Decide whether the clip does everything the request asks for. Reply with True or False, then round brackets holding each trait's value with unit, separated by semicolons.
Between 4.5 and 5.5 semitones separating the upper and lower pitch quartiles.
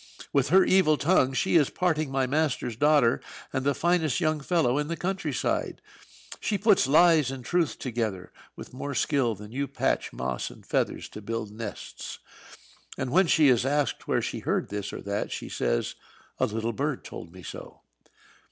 True (5.2 semitones)